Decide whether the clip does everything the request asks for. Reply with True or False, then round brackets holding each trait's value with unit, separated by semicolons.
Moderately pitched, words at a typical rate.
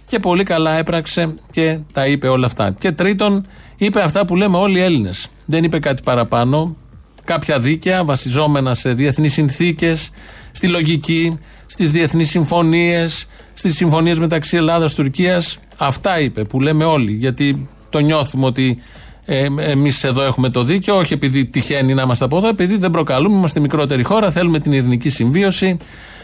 True (155 Hz; 160 wpm)